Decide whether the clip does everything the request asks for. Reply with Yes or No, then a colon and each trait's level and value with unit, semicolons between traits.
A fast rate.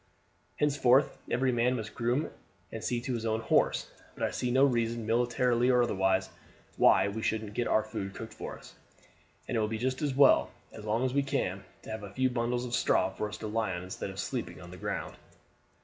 Yes: fast, 220 wpm